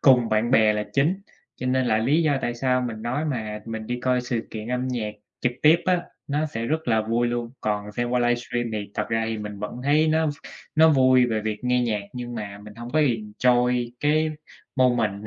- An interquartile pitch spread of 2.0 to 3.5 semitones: Yes, average, 2.9 semitones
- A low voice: Yes, low, 120 Hz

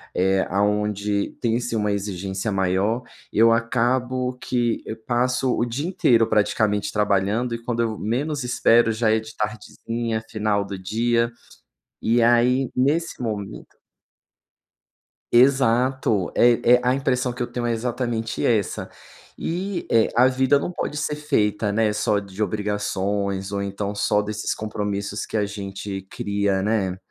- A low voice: Yes, low, 110 Hz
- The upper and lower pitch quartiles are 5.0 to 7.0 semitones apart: No, average, 3.2 semitones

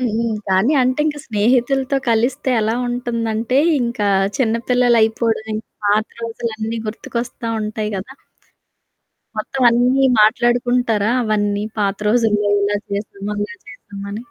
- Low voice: No, high, 225 Hz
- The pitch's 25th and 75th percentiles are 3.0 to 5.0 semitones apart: No, narrow, 2.5 semitones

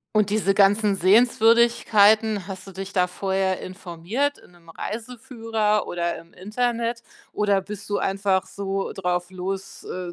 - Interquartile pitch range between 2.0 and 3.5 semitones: Yes, average, 2.7 semitones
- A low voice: No, high, 200 Hz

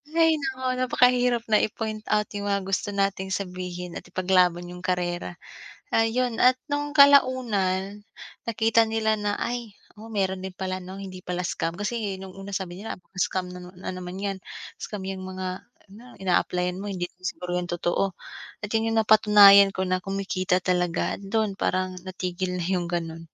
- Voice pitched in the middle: No, high, 195 Hz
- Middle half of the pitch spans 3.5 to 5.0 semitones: No, average, 3.1 semitones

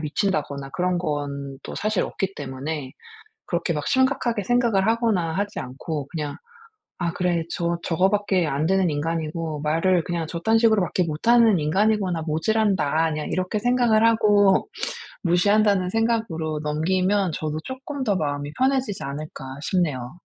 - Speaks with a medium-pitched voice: Yes, medium, 175 Hz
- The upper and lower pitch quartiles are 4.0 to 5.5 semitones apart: Yes, average, 5.2 semitones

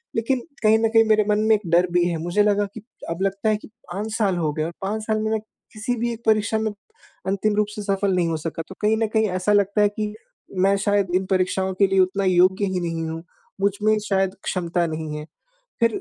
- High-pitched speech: Yes, high, 200 Hz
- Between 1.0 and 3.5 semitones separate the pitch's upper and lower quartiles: Yes, average, 2.9 semitones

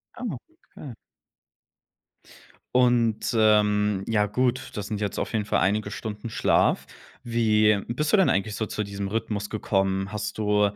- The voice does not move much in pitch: Yes, narrow, 1.8 semitones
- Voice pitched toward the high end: No, low, 105 Hz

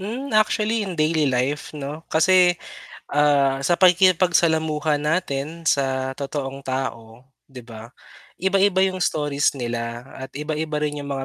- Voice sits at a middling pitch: Yes, medium, 150 Hz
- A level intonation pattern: No, average, 4.7 semitones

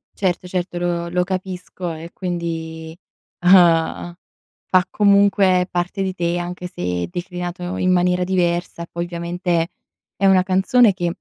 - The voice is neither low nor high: Yes, medium, 180 Hz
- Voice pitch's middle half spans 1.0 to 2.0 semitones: Yes, narrow, 1.3 semitones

